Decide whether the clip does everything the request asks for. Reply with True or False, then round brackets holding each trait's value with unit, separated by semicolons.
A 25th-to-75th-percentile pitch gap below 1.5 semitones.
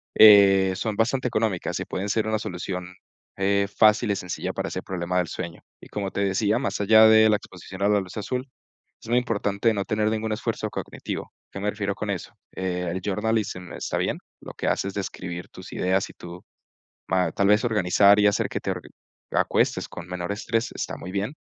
False (2.8 semitones)